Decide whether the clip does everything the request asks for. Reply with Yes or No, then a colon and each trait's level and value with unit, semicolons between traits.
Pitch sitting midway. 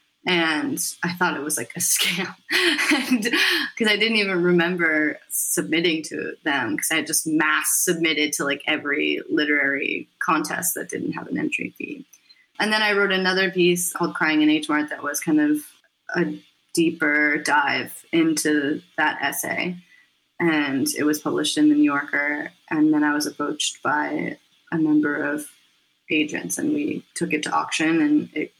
Yes: medium, 160 Hz